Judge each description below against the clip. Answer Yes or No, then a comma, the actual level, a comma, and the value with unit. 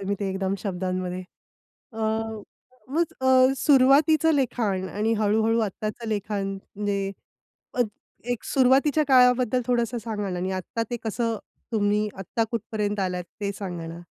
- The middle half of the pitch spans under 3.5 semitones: No, average, 3.8 semitones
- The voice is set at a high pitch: Yes, high, 215 Hz